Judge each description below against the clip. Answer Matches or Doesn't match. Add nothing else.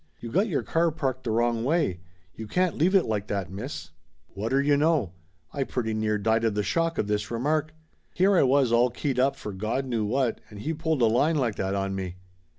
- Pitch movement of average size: Doesn't match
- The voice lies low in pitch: Matches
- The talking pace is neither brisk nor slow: Doesn't match